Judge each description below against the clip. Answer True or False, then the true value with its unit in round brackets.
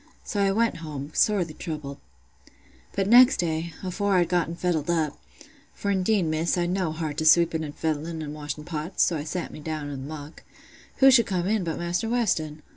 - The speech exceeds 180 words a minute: True (190 wpm)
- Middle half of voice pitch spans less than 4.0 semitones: True (3.6 semitones)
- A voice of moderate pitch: True (165 Hz)